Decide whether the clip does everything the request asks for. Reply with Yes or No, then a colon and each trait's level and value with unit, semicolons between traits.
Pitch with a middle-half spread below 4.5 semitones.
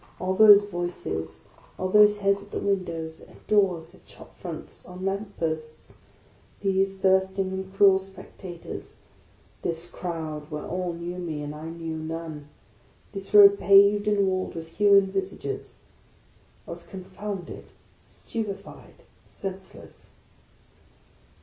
Yes: average, 3.2 semitones